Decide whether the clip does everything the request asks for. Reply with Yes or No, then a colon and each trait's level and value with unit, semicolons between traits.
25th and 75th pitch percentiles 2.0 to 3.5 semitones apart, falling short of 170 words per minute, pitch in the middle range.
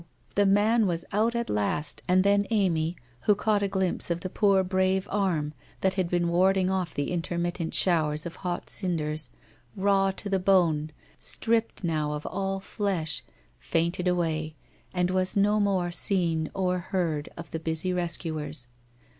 Yes: average, 2.9 semitones; average, 160 wpm; medium, 180 Hz